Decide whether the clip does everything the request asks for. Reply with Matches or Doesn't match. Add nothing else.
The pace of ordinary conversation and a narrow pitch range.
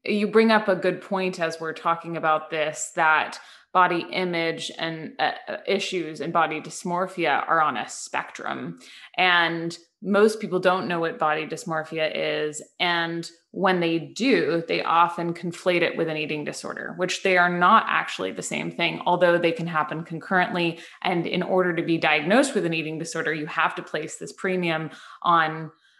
Matches